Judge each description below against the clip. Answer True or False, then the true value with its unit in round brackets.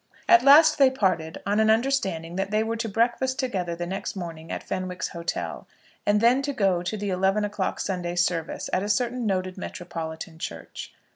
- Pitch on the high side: True (195 Hz)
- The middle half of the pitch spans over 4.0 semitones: True (4.6 semitones)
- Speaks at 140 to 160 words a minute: False (185 wpm)